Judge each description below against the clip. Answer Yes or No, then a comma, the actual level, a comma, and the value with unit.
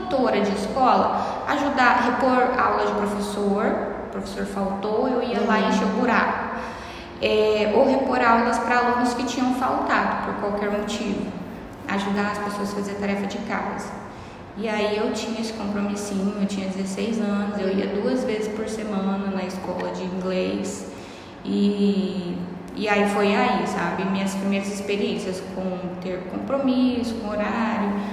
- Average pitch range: No, narrow, 2.1 semitones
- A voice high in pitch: Yes, high, 205 Hz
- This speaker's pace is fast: No, average, 155 wpm